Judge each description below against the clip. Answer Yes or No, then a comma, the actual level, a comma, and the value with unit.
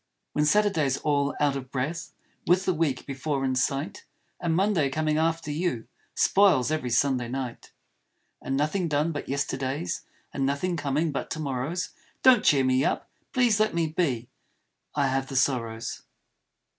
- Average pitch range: Yes, average, 3.8 semitones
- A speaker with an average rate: Yes, average, 160 wpm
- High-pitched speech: No, medium, 145 Hz